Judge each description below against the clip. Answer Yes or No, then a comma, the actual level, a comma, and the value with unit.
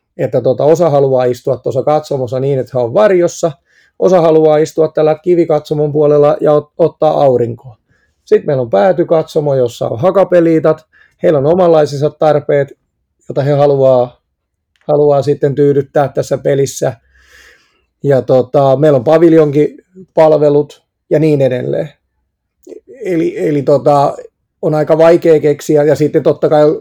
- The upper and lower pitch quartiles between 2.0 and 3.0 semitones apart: Yes, narrow, 2.4 semitones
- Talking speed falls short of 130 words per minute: No, average, 135 wpm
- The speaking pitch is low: No, medium, 150 Hz